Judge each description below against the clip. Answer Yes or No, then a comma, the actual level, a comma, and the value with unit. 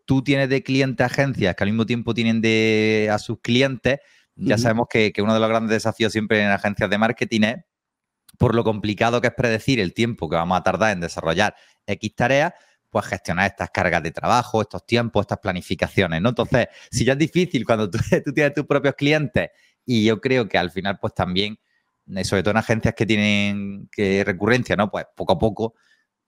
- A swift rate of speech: Yes, fast, 205 wpm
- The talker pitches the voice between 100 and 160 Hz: Yes, low, 110 Hz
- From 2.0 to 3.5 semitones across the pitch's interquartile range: Yes, average, 3.1 semitones